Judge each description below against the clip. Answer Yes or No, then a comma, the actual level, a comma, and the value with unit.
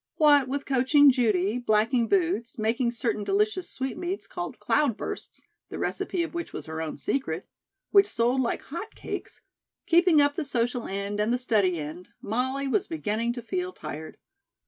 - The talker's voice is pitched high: Yes, very high, 250 Hz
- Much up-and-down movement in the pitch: Yes, wide, 5.8 semitones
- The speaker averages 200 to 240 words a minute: No, average, 165 wpm